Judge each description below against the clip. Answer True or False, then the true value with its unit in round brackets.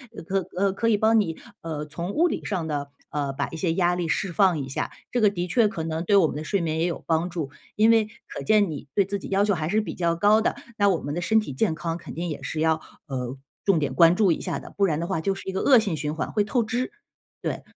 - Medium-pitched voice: True (175 Hz)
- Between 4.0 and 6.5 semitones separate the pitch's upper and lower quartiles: True (4.3 semitones)